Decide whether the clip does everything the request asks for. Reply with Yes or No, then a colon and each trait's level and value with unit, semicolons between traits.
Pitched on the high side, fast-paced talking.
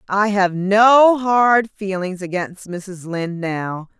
No: high, 195 Hz; slow, 135 wpm